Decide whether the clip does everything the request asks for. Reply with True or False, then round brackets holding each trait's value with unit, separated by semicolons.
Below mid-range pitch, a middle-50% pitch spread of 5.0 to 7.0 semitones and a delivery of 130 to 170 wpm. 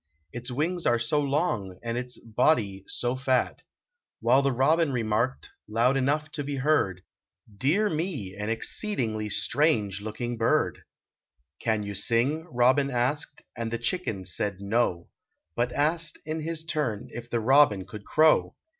True (125 Hz; 5.5 semitones; 155 wpm)